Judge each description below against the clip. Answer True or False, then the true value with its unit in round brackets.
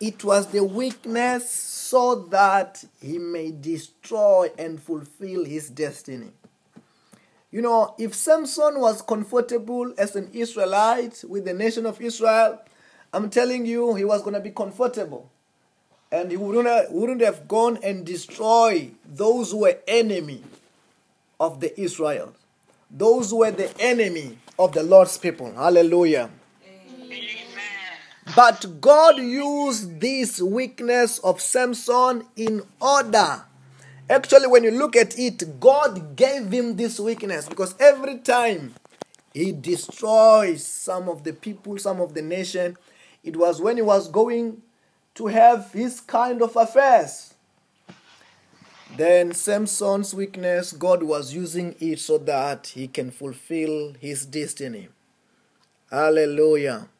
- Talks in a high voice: True (205 Hz)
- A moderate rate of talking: False (125 wpm)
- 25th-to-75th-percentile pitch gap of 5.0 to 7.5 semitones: True (5.4 semitones)